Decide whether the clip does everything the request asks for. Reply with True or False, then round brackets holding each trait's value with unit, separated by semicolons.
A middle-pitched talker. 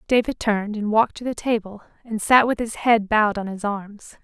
False (215 Hz)